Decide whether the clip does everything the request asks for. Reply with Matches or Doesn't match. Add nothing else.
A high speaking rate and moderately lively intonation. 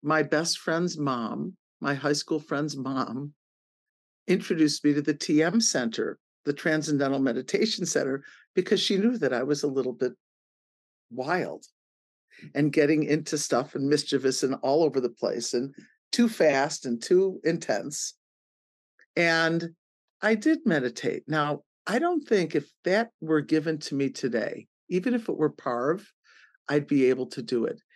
Doesn't match